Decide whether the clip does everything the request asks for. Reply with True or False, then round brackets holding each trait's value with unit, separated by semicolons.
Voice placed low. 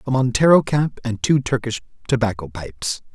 True (125 Hz)